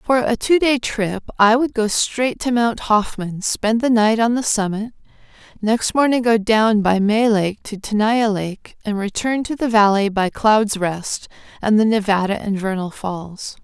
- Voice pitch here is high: Yes, high, 215 Hz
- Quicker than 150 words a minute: Yes, average, 185 wpm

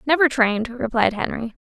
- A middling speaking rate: Yes, average, 150 wpm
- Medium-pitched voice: No, high, 245 Hz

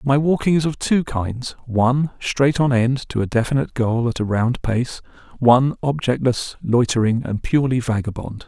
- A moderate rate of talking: Yes, average, 170 wpm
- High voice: No, low, 125 Hz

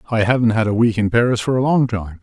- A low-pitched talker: Yes, low, 115 Hz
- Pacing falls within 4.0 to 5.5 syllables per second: No, 6.5 syllables/s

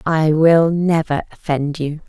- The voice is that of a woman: Yes, female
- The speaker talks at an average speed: Yes, average, 145 wpm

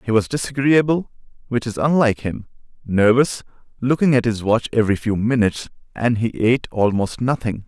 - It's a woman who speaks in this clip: No, male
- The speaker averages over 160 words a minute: No, average, 155 wpm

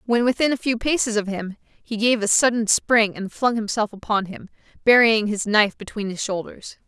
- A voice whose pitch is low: No, high, 220 Hz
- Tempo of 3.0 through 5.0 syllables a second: No, 5.2 syllables/s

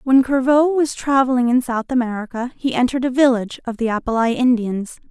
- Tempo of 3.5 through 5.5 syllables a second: No, 5.9 syllables/s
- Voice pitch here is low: No, very high, 250 Hz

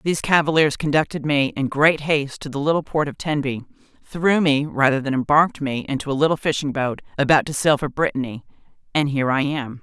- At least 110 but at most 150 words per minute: No, average, 200 wpm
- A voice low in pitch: No, medium, 145 Hz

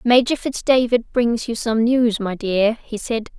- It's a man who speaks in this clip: No, female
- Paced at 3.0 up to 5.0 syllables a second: Yes, 4.1 syllables/s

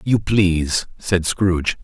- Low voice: Yes, very low, 90 Hz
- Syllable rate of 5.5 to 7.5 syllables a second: No, 4.4 syllables/s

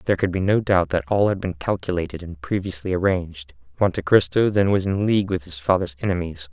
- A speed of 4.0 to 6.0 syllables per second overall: No, 6.2 syllables/s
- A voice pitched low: Yes, very low, 90 Hz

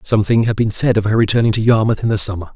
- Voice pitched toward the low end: Yes, low, 110 Hz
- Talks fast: Yes, fast, 280 wpm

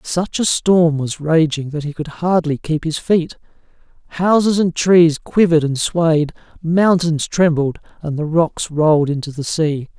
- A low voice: No, medium, 160 Hz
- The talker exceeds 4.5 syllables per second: No, 4.2 syllables/s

